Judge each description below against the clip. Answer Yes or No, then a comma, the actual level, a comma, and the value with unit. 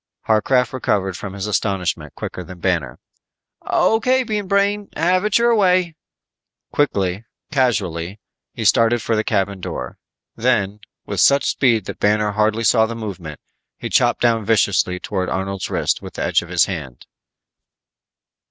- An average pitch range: No, wide, 5.9 semitones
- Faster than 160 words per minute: No, average, 150 wpm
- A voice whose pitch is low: Yes, low, 110 Hz